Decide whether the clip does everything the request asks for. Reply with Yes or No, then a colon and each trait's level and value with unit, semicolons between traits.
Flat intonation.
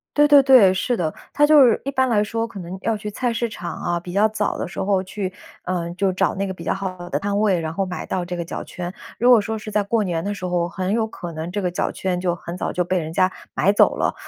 No: average, 3.5 semitones